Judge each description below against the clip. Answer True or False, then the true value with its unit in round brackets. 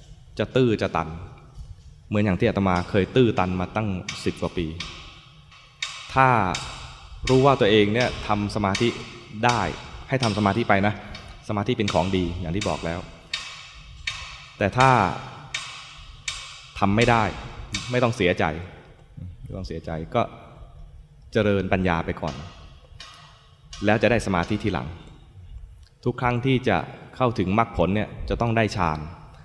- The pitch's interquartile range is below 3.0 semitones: False (5.2 semitones)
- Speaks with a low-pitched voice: True (100 Hz)